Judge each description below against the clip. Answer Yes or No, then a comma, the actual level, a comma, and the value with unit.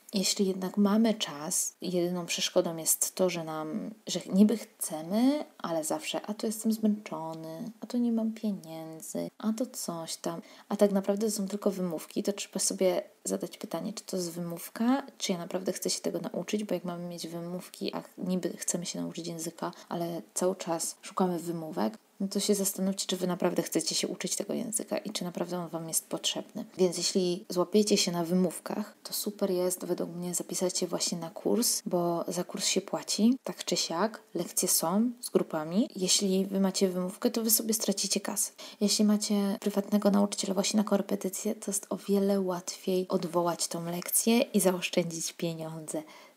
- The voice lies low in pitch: No, high, 190 Hz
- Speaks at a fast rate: Yes, fast, 180 wpm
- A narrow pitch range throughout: No, average, 3.0 semitones